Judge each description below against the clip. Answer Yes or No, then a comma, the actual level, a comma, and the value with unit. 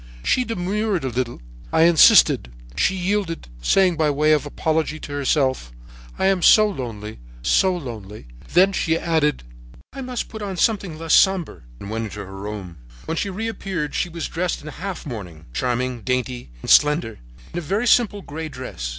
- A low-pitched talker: No, medium, 155 Hz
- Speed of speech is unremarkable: Yes, average, 170 wpm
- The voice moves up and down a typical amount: No, wide, 7.7 semitones